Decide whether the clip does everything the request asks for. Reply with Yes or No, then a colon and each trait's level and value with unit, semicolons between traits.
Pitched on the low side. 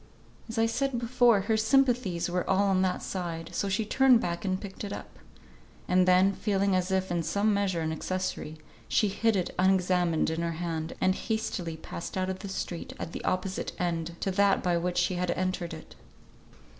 No: medium, 185 Hz